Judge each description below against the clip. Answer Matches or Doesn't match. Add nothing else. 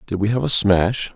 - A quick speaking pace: Matches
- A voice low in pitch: Matches